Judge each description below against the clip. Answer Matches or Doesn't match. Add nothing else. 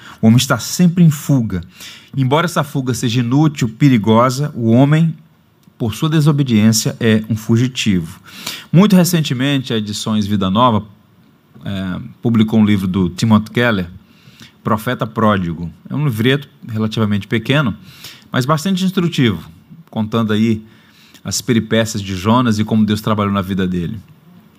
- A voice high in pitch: Doesn't match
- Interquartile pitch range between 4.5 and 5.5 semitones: Matches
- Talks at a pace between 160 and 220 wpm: Doesn't match